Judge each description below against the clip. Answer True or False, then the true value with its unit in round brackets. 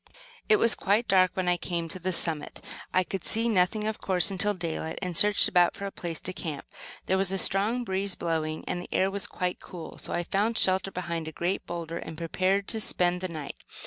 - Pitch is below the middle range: False (185 Hz)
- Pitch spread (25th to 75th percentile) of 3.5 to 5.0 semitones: False (2.5 semitones)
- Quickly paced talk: True (230 wpm)